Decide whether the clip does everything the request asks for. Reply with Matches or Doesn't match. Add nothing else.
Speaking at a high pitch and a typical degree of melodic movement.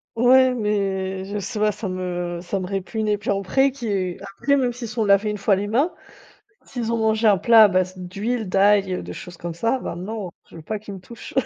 Matches